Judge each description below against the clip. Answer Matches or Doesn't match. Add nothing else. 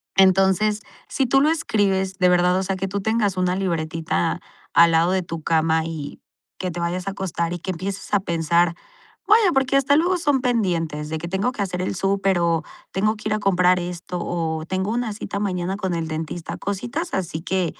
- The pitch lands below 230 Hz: Matches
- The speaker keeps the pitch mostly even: Doesn't match